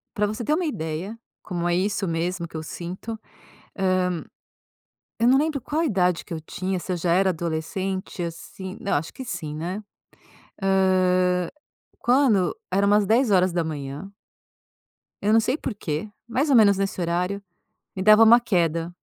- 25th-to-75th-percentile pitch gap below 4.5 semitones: Yes, average, 3.8 semitones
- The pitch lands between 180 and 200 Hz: Yes, high, 190 Hz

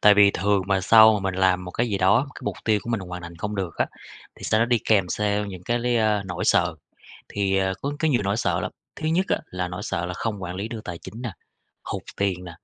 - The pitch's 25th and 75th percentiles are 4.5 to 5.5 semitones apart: No, average, 3.2 semitones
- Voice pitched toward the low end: Yes, low, 100 Hz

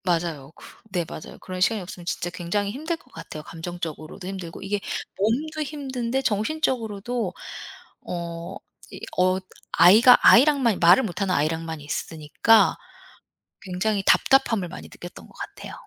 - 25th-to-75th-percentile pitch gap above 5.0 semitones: Yes, wide, 5.4 semitones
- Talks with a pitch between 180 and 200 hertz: Yes, high, 190 Hz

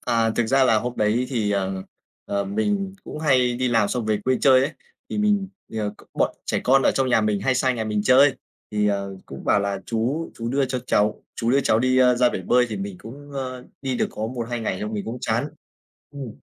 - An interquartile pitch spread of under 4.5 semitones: Yes, average, 3.6 semitones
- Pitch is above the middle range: No, low, 120 Hz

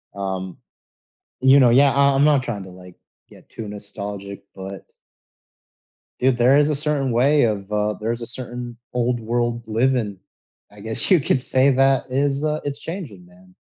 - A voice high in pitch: No, low, 120 Hz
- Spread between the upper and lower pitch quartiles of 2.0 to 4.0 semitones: No, average, 4.8 semitones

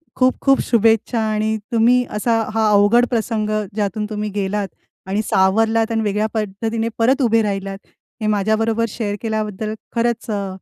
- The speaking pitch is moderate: No, high, 220 Hz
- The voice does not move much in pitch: Yes, narrow, 1.7 semitones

